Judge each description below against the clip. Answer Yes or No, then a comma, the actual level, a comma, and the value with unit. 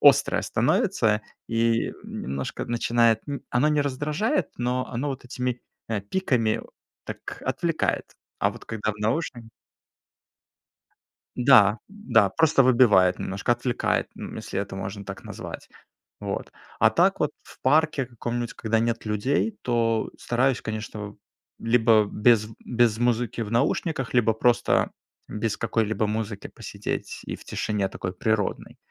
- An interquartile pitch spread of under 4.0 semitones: Yes, average, 2.8 semitones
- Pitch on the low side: Yes, low, 115 Hz